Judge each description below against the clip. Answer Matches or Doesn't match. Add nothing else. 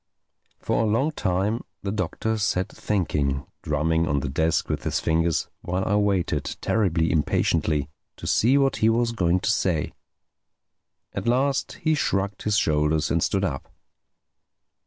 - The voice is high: Doesn't match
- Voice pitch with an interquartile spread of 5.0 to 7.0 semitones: Matches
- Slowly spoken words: Doesn't match